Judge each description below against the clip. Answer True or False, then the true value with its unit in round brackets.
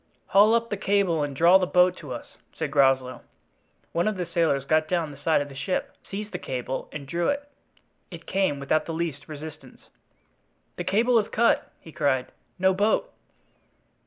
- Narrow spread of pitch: False (5.1 semitones)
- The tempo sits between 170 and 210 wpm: True (185 wpm)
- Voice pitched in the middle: True (170 Hz)